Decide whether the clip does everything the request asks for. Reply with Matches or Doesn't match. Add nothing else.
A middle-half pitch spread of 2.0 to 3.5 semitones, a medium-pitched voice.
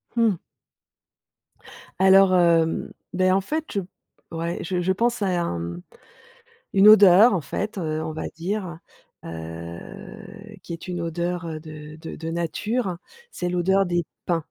Matches